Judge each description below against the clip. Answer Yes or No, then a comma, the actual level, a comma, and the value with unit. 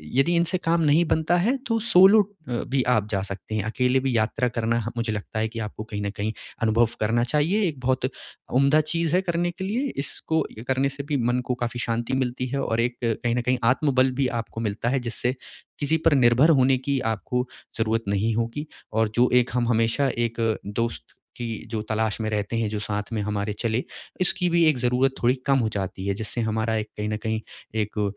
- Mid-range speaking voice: No, low, 120 Hz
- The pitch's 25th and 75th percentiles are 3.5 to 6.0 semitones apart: Yes, average, 4.1 semitones